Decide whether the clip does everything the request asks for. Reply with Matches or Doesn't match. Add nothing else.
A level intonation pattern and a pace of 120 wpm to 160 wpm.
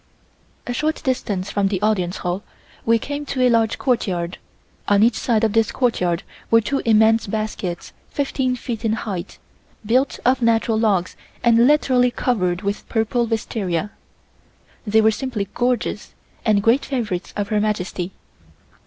Doesn't match